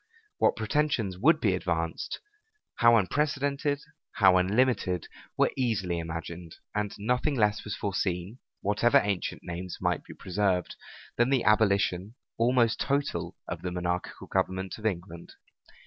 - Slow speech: Yes, slow, 130 wpm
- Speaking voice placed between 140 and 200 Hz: No, low, 100 Hz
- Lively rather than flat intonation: No, average, 5.0 semitones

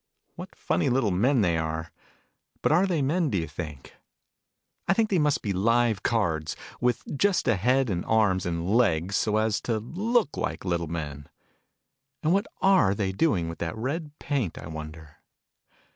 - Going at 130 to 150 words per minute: No, average, 175 wpm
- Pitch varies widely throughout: Yes, wide, 8.7 semitones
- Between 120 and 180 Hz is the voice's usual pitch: No, low, 105 Hz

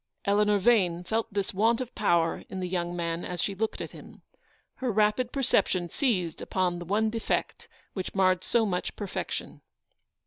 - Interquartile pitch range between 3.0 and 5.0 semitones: Yes, average, 3.7 semitones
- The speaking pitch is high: Yes, high, 195 Hz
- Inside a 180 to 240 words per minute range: No, average, 170 wpm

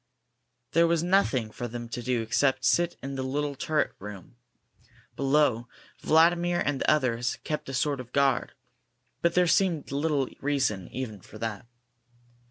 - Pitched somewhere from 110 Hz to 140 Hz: Yes, low, 135 Hz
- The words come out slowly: No, average, 155 wpm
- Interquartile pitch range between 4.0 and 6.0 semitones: Yes, average, 4.5 semitones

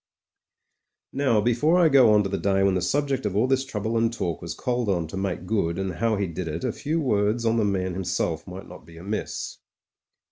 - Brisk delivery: Yes, fast, 240 wpm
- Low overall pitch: Yes, low, 100 Hz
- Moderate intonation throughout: Yes, average, 4.5 semitones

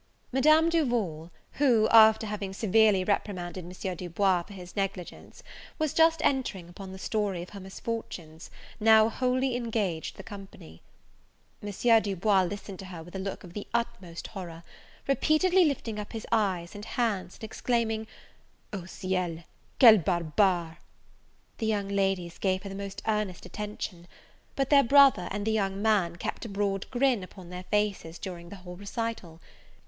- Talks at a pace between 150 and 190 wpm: Yes, average, 160 wpm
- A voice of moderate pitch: No, high, 200 Hz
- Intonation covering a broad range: No, average, 3.6 semitones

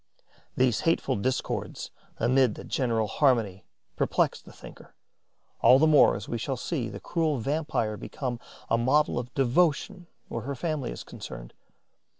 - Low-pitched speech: Yes, low, 130 Hz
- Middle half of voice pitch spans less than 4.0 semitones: No, average, 4.6 semitones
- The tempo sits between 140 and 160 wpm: Yes, average, 150 wpm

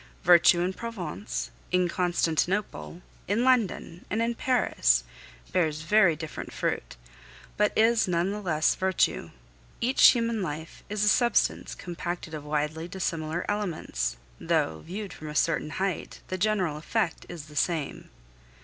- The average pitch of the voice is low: No, medium, 175 Hz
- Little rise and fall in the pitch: No, average, 4.9 semitones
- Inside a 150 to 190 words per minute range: No, average, 140 wpm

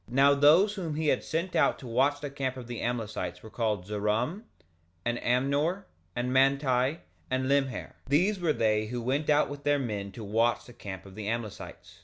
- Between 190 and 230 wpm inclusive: Yes, average, 200 wpm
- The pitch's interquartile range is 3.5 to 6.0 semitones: Yes, average, 4.3 semitones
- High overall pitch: No, low, 130 Hz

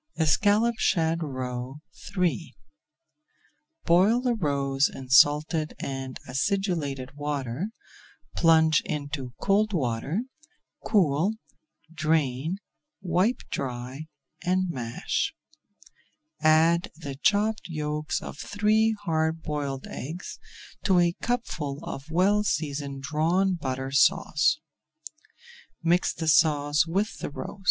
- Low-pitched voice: No, medium, 155 Hz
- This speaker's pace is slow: Yes, slow, 100 wpm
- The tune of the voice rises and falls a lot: No, average, 4.8 semitones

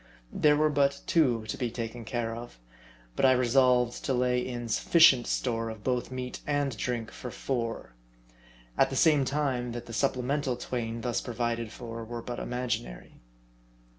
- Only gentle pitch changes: Yes, narrow, 2.1 semitones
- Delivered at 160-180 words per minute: Yes, average, 165 wpm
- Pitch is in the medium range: No, low, 125 Hz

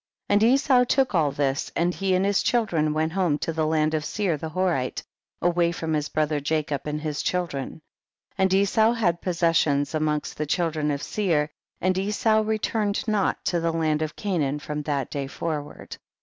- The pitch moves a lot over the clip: No, average, 4.2 semitones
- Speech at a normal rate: Yes, average, 190 wpm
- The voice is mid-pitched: Yes, medium, 165 Hz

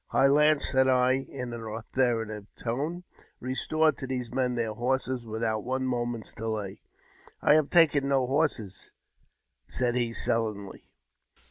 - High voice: No, low, 125 Hz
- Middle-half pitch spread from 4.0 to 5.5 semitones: No, average, 2.9 semitones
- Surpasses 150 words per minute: No, average, 140 wpm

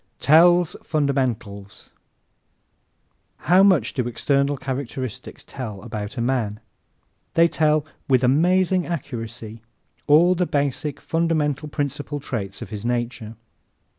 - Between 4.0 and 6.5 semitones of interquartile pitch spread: Yes, average, 4.9 semitones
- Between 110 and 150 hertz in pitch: Yes, medium, 140 Hz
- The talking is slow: Yes, slow, 110 wpm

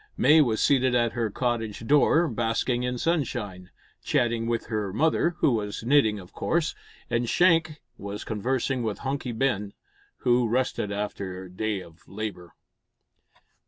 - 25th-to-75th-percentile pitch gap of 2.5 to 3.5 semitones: No, average, 4.1 semitones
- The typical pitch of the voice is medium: No, low, 115 Hz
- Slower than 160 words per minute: Yes, average, 145 wpm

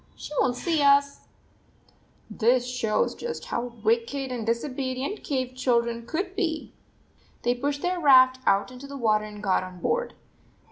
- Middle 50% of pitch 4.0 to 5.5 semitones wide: No, average, 3.3 semitones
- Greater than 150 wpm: Yes, average, 170 wpm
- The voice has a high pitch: Yes, very high, 255 Hz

